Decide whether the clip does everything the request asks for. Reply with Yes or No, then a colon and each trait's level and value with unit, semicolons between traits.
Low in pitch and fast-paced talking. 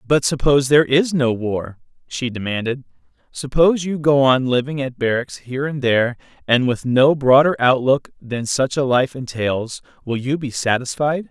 No: low, 130 Hz; average, 170 wpm